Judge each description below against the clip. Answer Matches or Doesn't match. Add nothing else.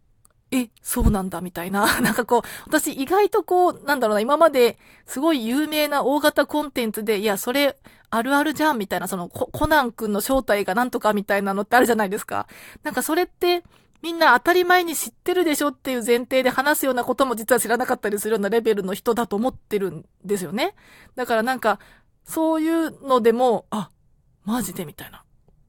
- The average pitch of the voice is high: Matches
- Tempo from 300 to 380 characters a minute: Doesn't match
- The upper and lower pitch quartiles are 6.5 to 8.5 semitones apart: Doesn't match